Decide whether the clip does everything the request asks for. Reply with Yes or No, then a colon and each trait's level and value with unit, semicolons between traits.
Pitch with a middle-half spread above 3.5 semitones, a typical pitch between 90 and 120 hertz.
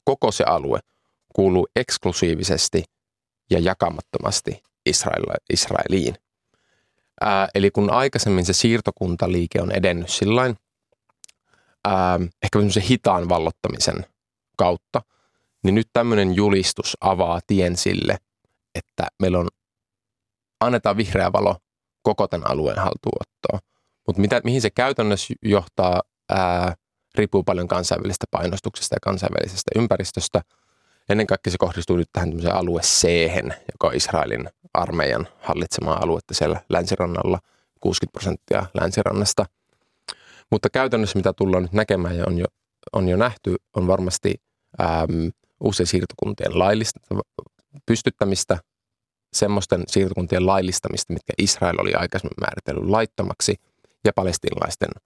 No: average, 3.0 semitones; very low, 95 Hz